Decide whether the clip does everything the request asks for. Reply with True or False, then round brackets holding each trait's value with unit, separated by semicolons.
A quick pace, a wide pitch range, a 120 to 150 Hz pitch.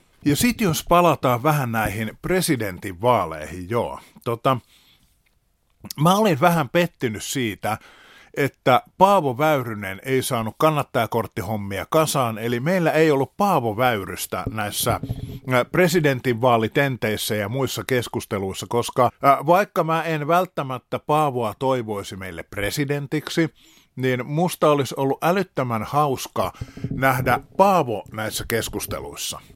False (105 wpm; 5.8 semitones; 130 Hz)